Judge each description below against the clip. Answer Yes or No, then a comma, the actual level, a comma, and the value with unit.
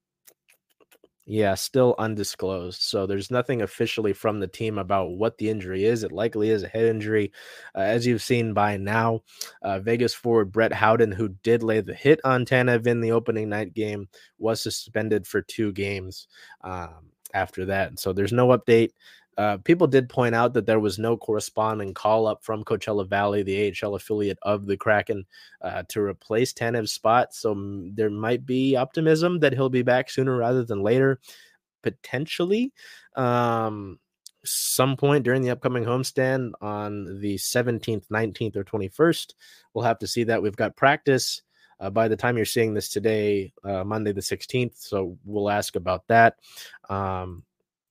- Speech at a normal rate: Yes, average, 170 wpm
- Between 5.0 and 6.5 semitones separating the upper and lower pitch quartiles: No, average, 3.2 semitones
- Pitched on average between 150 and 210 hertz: No, low, 110 Hz